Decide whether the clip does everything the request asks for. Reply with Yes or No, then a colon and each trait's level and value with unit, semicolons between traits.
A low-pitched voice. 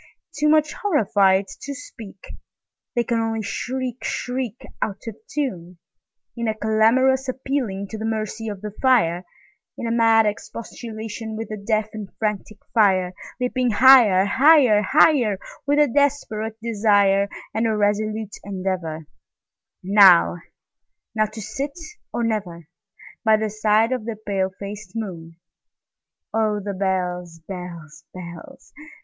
No: high, 215 Hz